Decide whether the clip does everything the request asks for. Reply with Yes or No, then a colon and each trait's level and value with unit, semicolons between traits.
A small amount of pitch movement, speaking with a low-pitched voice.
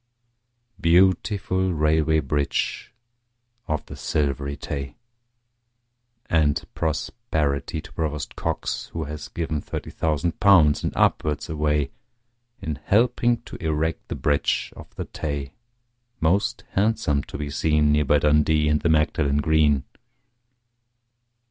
Yes: narrow, 1.9 semitones; very low, 75 Hz